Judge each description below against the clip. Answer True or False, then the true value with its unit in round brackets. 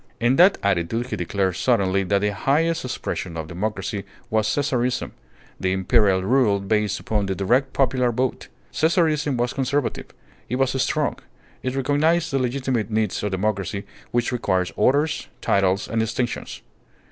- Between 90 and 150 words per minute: True (145 wpm)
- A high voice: False (115 Hz)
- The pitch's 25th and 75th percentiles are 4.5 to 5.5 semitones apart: True (5.1 semitones)